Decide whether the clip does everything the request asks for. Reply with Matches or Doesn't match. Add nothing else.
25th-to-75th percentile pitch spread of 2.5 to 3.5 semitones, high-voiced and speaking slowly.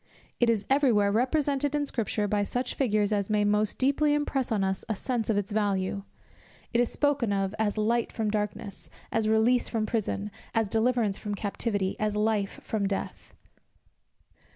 Doesn't match